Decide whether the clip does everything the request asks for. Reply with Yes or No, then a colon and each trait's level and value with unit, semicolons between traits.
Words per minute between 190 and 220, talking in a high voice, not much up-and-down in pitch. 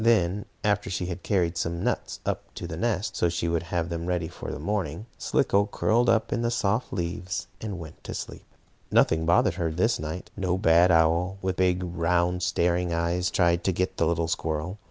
No: average, 200 wpm; very low, 90 Hz; narrow, 2.2 semitones